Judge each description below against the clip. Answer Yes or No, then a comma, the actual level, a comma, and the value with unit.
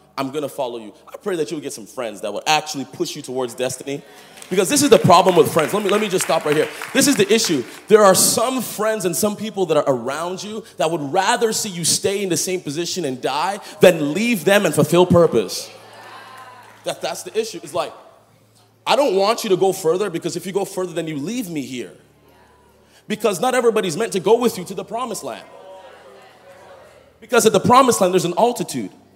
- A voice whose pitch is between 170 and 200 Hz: Yes, high, 190 Hz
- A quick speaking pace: Yes, fast, 225 wpm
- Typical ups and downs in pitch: Yes, average, 4.9 semitones